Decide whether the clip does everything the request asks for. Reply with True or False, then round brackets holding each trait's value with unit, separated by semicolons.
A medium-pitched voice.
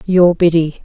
True (170 Hz)